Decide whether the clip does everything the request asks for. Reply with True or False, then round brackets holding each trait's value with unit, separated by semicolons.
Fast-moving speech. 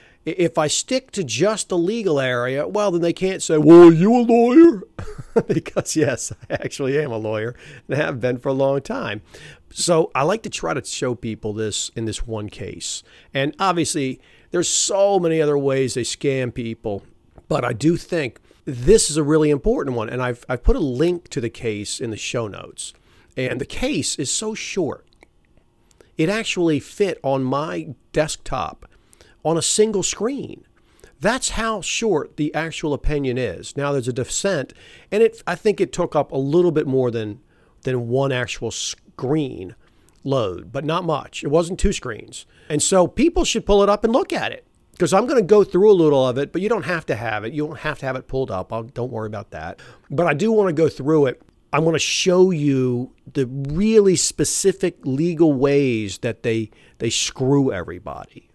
False (195 wpm)